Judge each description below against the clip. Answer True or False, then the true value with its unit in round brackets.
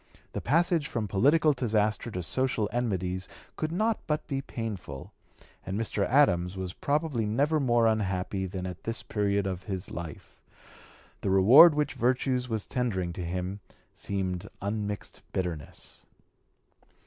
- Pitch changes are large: True (5.7 semitones)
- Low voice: True (105 Hz)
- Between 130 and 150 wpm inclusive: True (135 wpm)